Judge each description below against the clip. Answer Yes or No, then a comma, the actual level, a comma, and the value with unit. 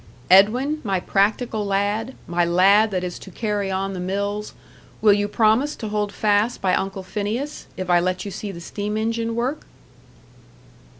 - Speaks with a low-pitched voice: No, high, 205 Hz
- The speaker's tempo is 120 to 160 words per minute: No, average, 170 wpm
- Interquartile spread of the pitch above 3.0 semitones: No, narrow, 2.4 semitones